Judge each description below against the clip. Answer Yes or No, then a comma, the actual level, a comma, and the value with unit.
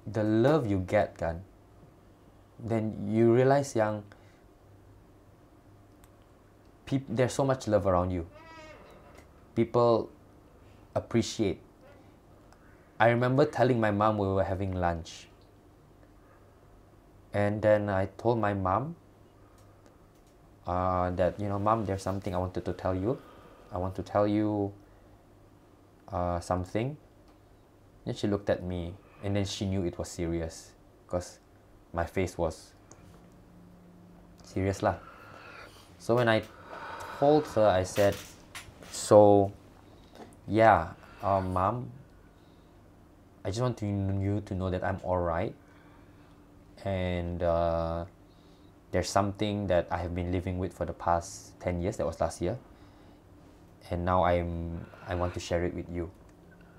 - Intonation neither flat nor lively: No, narrow, 2.2 semitones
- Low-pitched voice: Yes, low, 100 Hz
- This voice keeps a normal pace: Yes, average, 125 wpm